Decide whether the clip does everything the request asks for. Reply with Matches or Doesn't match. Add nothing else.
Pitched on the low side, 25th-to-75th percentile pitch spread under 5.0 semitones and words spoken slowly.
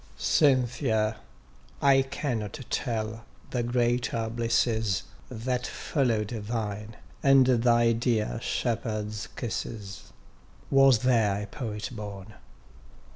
Matches